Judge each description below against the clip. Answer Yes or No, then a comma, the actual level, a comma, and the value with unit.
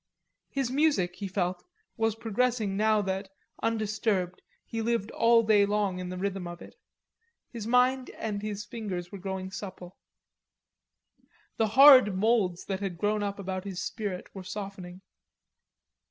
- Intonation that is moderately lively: Yes, average, 3.1 semitones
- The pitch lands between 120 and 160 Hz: No, high, 205 Hz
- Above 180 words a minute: No, average, 145 wpm